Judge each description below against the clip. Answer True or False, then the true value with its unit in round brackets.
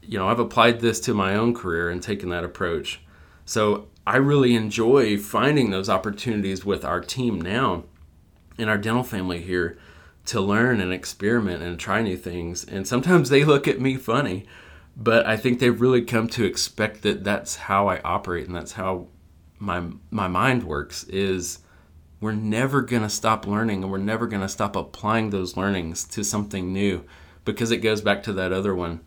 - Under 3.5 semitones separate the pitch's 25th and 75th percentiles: False (4.4 semitones)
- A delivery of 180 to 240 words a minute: True (190 wpm)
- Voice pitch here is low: True (100 Hz)